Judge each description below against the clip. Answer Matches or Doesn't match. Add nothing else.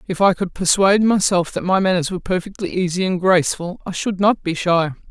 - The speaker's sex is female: Matches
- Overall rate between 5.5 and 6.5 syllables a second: Matches